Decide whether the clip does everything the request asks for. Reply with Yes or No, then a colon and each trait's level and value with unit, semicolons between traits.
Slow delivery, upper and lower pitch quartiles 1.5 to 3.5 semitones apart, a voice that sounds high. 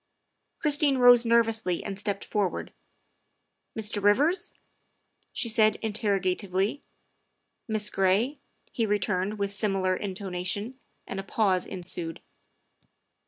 Yes: slow, 110 wpm; average, 3.0 semitones; high, 205 Hz